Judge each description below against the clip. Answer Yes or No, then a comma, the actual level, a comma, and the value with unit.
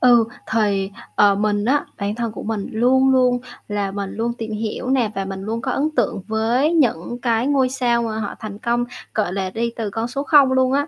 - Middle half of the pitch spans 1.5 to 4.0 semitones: Yes, average, 3.6 semitones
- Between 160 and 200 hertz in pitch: No, high, 230 Hz